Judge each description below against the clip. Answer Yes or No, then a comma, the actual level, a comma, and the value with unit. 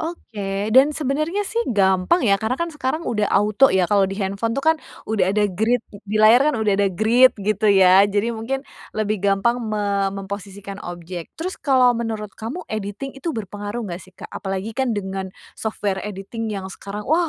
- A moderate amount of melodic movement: Yes, average, 3.8 semitones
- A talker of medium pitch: No, high, 210 Hz